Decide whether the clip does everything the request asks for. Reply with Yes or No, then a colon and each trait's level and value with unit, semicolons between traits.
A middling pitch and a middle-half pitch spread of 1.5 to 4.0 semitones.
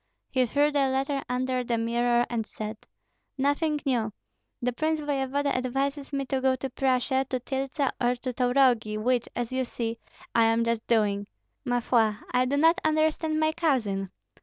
No: very high, 255 Hz; average, 2.9 semitones